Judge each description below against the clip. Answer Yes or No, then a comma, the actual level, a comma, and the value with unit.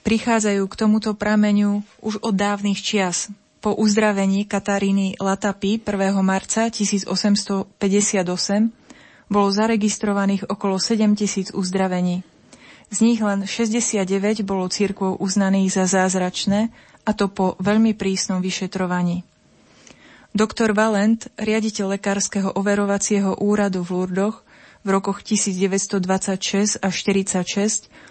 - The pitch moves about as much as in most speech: No, narrow, 1.7 semitones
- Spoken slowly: Yes, slow, 100 wpm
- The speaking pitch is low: No, high, 200 Hz